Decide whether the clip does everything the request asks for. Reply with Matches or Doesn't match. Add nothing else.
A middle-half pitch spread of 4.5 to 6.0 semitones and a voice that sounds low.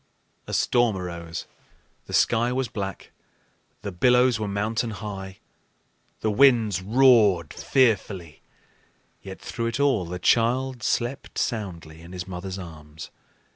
Matches